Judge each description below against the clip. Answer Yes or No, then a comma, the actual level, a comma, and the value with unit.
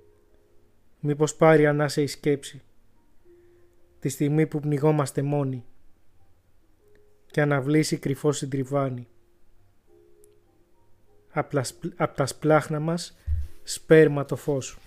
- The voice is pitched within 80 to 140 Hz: Yes, low, 135 Hz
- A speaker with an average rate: No, slow, 85 wpm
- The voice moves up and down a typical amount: No, wide, 6.8 semitones